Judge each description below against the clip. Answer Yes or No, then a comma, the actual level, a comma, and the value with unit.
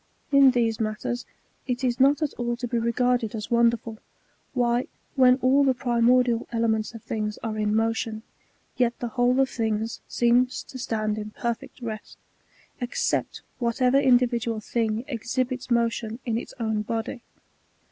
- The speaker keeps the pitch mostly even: Yes, narrow, 2.0 semitones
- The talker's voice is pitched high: Yes, high, 235 Hz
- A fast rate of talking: No, average, 155 wpm